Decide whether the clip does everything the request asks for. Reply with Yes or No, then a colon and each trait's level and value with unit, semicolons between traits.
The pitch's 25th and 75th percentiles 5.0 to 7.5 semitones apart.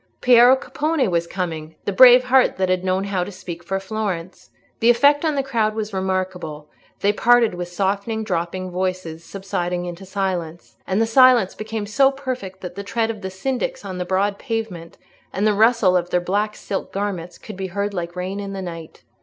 No: average, 3.8 semitones